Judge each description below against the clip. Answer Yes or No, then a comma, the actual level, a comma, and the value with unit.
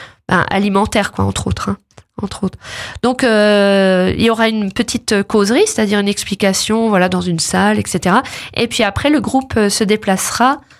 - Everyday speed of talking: Yes, average, 170 wpm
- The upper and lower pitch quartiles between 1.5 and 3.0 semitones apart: Yes, narrow, 2.6 semitones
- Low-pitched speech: No, high, 210 Hz